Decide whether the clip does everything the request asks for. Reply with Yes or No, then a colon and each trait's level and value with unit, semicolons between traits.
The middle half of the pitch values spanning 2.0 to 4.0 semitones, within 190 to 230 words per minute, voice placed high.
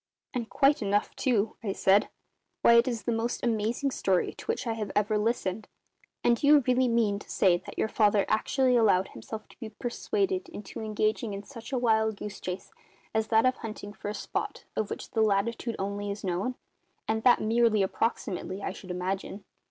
Yes: average, 2.8 semitones; average, 195 wpm; high, 220 Hz